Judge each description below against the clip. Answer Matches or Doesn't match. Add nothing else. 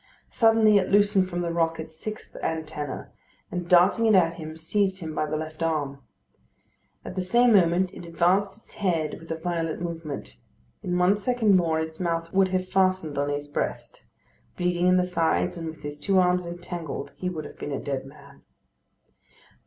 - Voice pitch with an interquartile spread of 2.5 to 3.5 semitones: Matches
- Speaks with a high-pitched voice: Doesn't match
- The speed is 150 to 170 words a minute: Doesn't match